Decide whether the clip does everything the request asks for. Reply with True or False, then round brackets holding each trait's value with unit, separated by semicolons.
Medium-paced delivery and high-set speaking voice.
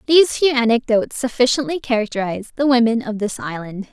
True (155 wpm; 240 Hz)